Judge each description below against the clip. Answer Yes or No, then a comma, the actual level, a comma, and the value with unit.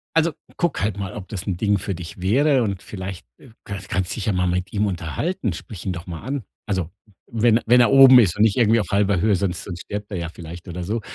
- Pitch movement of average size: Yes, average, 3.8 semitones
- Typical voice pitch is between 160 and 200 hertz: No, low, 100 Hz